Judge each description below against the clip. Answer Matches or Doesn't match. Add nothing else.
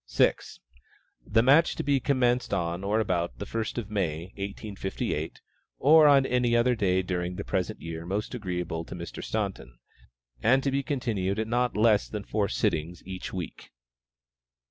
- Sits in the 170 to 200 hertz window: Doesn't match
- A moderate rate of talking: Matches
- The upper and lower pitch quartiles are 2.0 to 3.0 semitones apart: Doesn't match